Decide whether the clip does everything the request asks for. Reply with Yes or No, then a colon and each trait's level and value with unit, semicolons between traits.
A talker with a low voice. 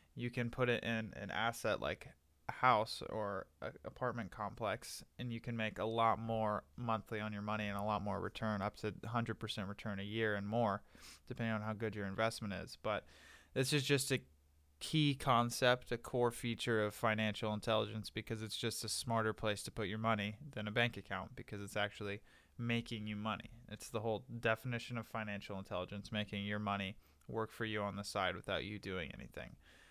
Yes: low, 110 Hz